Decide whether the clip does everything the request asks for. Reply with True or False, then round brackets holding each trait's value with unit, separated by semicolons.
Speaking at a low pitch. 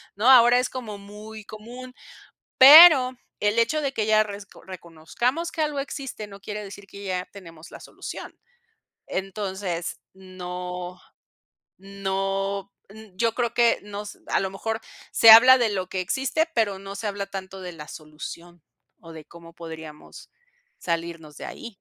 False (200 Hz)